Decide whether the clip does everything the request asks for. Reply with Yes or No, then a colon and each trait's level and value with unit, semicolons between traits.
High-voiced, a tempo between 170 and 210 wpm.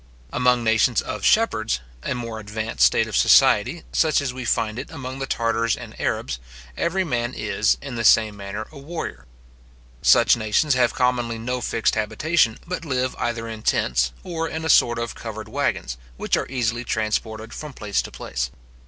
No: low, 115 Hz; average, 180 wpm